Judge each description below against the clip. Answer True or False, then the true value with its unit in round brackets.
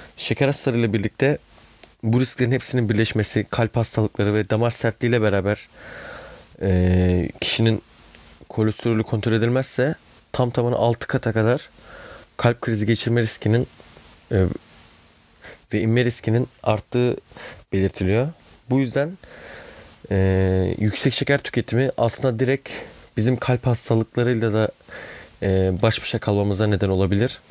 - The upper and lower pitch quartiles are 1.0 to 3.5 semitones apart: True (3.0 semitones)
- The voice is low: True (115 Hz)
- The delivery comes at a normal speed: True (115 wpm)